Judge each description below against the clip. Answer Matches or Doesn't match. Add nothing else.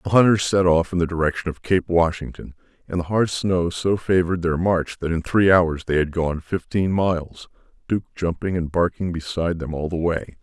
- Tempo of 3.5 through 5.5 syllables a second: Matches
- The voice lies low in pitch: Matches